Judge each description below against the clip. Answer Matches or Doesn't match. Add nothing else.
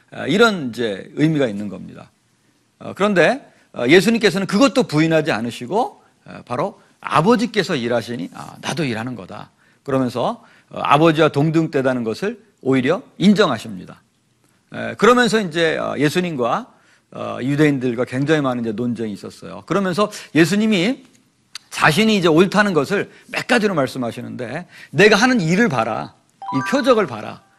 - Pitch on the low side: Doesn't match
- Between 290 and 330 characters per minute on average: Matches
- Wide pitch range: Matches